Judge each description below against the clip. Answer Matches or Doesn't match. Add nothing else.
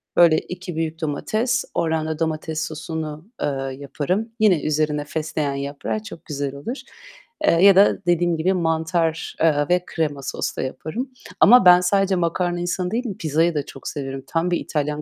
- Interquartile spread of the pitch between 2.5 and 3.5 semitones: Matches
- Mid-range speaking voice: Matches